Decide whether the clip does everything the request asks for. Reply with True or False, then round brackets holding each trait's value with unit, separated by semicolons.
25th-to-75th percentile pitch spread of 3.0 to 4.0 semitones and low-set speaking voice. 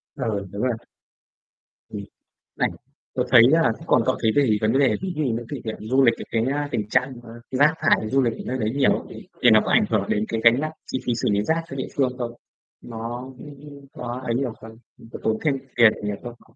True (3.4 semitones; 120 Hz)